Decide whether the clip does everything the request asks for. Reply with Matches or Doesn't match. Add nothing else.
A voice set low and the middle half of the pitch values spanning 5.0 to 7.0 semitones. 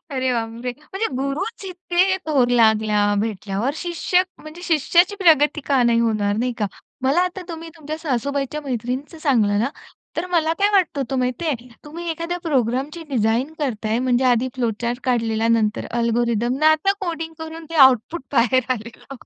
Doesn't match